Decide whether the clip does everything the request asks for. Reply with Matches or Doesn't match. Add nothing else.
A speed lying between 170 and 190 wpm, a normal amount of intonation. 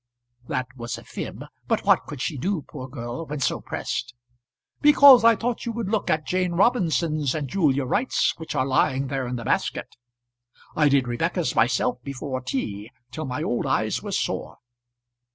Doesn't match